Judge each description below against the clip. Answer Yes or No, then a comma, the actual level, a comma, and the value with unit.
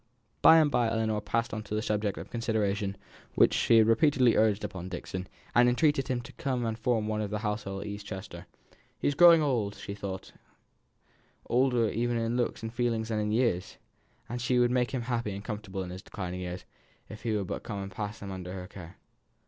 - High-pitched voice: No, low, 110 Hz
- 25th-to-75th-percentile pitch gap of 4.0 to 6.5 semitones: No, average, 3.3 semitones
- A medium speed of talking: No, fast, 220 wpm